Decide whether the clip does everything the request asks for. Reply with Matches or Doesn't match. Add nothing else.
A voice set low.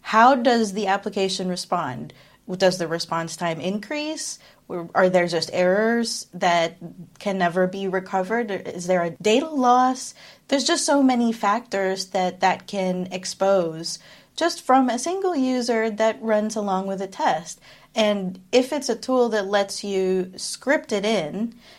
Doesn't match